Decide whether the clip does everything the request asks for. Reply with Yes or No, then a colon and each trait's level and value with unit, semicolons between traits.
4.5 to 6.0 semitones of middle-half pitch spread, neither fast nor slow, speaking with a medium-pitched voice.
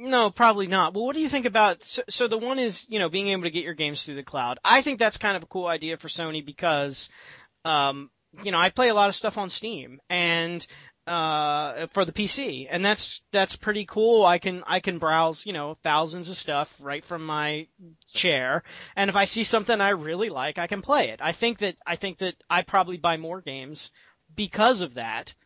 No: average, 4.8 semitones; fast, 230 wpm; medium, 180 Hz